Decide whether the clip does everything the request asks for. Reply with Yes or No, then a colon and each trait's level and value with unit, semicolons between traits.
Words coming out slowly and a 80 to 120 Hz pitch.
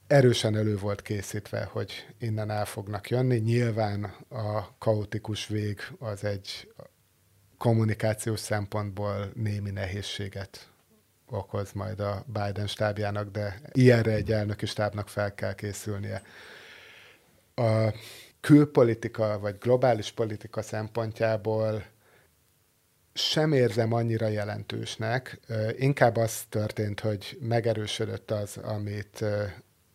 Yes: slow, 100 wpm; low, 110 Hz